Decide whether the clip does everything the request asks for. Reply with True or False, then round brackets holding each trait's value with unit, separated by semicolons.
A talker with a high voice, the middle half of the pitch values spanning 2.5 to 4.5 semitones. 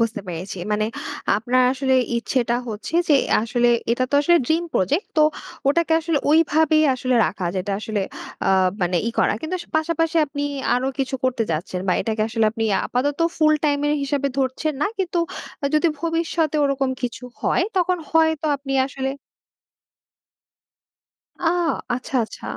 False (275 Hz; 5.3 semitones)